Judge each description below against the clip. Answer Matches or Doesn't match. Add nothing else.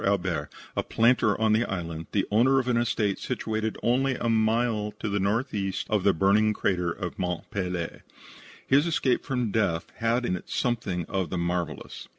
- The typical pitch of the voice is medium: Doesn't match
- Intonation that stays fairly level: Doesn't match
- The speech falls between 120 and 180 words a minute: Matches